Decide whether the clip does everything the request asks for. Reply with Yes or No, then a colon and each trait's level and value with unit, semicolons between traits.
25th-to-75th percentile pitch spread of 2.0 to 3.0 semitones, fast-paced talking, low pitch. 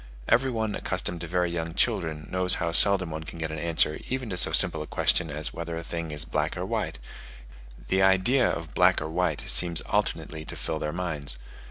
Yes: average, 2.7 semitones; fast, 210 wpm; very low, 85 Hz